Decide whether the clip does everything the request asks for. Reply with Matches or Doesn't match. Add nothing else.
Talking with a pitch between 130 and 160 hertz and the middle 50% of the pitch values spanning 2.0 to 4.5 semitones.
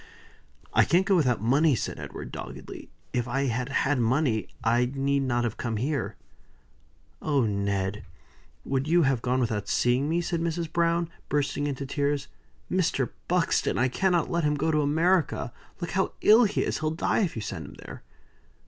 Doesn't match